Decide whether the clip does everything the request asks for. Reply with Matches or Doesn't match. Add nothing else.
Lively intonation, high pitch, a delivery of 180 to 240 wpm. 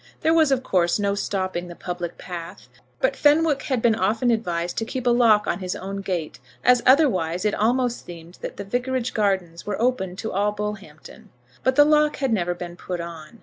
Matches